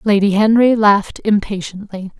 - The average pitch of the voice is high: Yes, high, 205 Hz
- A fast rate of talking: No, slow, 110 wpm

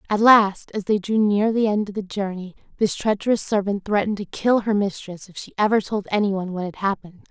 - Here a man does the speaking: No, female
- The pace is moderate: No, fast, 220 wpm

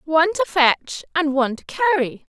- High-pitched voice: Yes, very high, 310 Hz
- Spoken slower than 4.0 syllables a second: No, 5.1 syllables/s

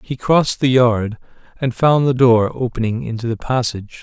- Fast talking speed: No, average, 180 wpm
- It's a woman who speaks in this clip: No, male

